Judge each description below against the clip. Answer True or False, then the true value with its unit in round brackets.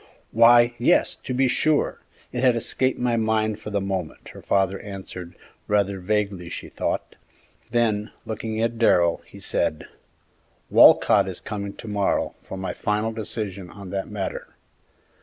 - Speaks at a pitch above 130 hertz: False (105 Hz)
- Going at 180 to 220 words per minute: False (150 wpm)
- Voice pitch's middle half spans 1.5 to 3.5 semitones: True (2.9 semitones)